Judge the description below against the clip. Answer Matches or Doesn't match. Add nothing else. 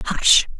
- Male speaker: Doesn't match